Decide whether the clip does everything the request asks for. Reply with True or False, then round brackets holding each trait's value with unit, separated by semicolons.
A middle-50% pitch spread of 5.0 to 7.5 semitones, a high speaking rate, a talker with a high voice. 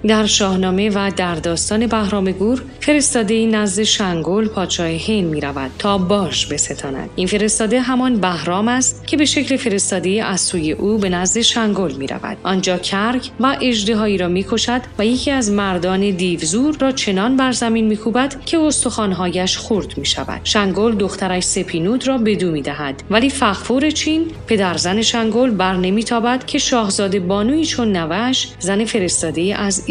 False (4.2 semitones; 165 wpm; 210 Hz)